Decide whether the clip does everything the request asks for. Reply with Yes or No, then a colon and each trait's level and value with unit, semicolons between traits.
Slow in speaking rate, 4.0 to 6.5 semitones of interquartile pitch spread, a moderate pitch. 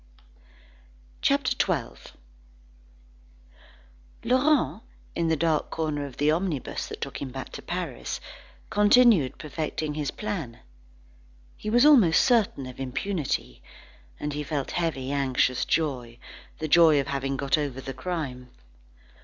Yes: slow, 125 wpm; average, 4.7 semitones; medium, 150 Hz